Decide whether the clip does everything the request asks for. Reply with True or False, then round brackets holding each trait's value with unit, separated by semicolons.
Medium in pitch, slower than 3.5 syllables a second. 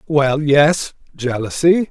True (150 Hz; 3.2 syllables/s)